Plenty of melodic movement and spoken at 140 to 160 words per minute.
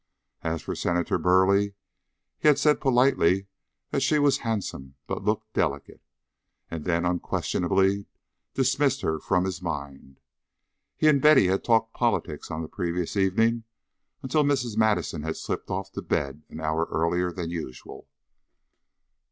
Yes: wide, 6.1 semitones; average, 145 wpm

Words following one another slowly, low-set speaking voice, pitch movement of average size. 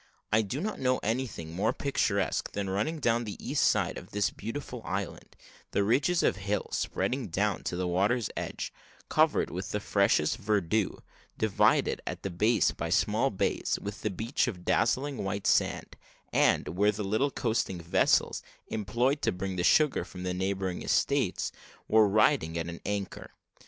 No: average, 165 wpm; low, 105 Hz; average, 3.9 semitones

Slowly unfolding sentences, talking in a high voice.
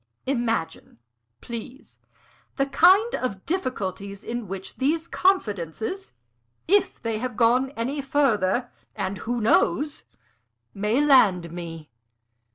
Yes: slow, 105 wpm; high, 235 Hz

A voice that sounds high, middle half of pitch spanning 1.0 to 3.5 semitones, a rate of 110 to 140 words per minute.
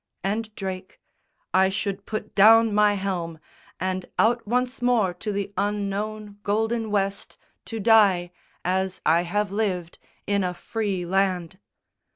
Yes: high, 200 Hz; narrow, 2.4 semitones; slow, 135 wpm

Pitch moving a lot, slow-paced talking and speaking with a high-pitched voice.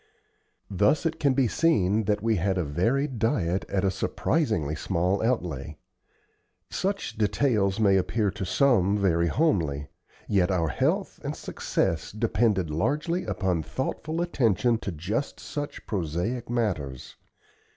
No: wide, 5.9 semitones; slow, 130 wpm; low, 100 Hz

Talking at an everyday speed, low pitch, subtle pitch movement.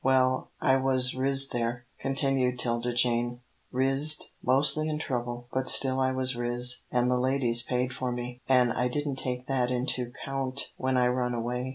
Yes: average, 175 wpm; low, 125 Hz; narrow, 1.4 semitones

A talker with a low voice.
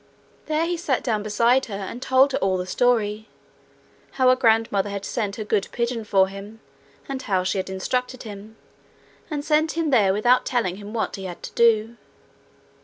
No: high, 225 Hz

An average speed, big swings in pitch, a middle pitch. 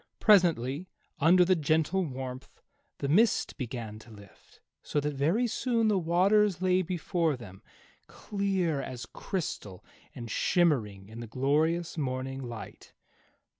No: slow, 130 wpm; wide, 6.3 semitones; medium, 155 Hz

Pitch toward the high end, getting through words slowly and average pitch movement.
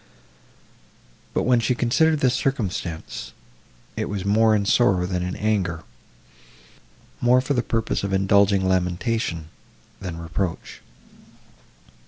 No: low, 100 Hz; slow, 110 wpm; average, 4.7 semitones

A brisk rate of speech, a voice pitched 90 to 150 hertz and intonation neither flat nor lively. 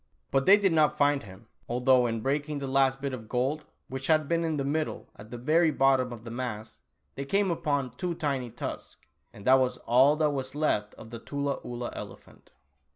Yes: fast, 210 wpm; low, 135 Hz; average, 3.5 semitones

